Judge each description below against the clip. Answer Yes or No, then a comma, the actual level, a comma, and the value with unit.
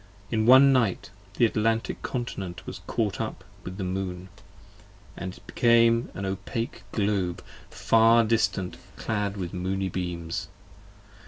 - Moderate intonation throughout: Yes, average, 3.6 semitones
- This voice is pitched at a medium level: No, low, 100 Hz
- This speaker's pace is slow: Yes, slow, 130 wpm